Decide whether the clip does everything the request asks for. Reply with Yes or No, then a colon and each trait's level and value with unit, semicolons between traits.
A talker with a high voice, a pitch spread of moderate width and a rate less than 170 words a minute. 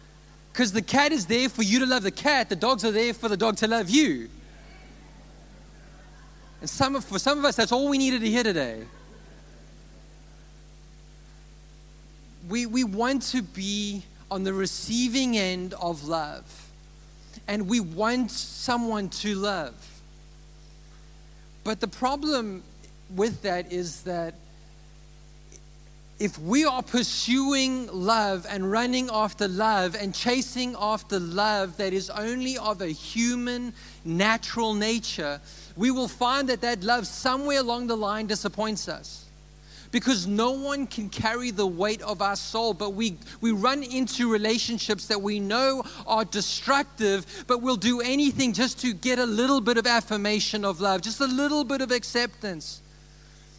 Yes: high, 220 Hz; average, 4.4 semitones; average, 150 wpm